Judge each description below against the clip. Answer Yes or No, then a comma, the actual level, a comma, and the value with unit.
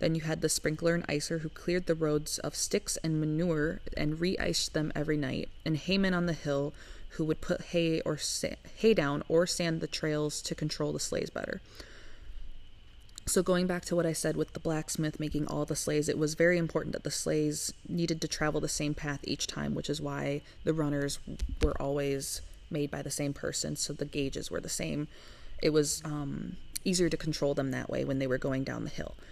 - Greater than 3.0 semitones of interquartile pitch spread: No, narrow, 2.5 semitones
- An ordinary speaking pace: No, fast, 215 wpm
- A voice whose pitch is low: No, medium, 150 Hz